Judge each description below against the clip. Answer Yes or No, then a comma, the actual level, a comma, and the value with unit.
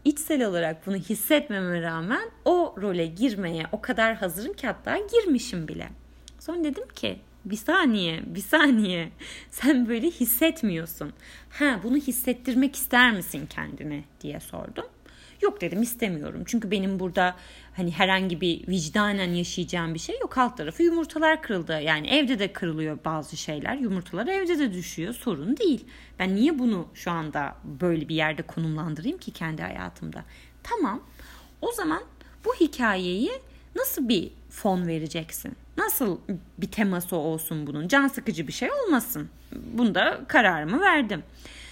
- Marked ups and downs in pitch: Yes, wide, 8.3 semitones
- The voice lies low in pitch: No, high, 210 Hz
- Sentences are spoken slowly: No, fast, 140 wpm